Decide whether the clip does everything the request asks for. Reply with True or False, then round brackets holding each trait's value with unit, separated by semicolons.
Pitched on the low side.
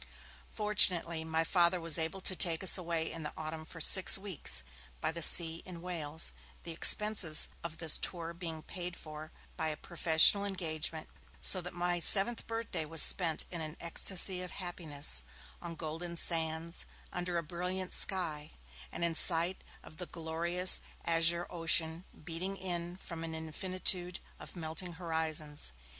False (170 Hz)